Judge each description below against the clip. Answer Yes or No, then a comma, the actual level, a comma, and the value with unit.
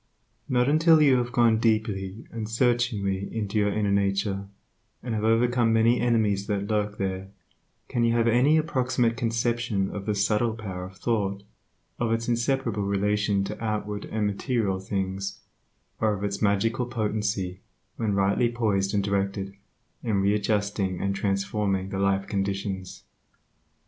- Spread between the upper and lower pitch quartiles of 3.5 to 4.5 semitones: No, average, 2.8 semitones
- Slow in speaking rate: No, average, 145 wpm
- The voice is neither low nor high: No, low, 105 Hz